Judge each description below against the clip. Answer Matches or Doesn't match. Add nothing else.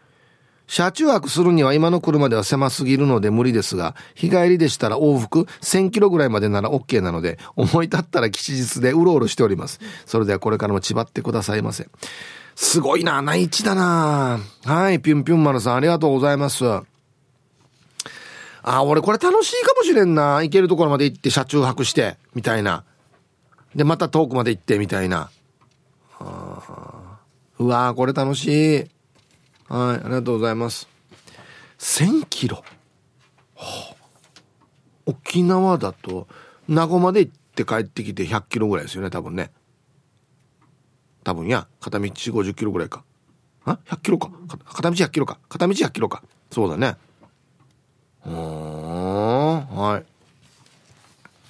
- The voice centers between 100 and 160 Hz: Matches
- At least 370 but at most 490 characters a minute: Doesn't match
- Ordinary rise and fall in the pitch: Matches